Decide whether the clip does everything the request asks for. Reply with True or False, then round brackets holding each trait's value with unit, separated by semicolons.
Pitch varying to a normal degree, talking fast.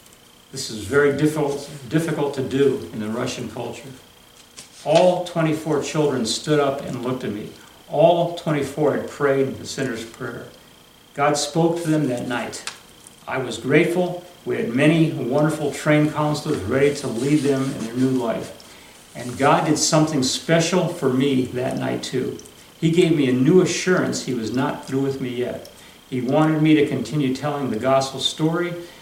False (3.0 semitones; 170 wpm)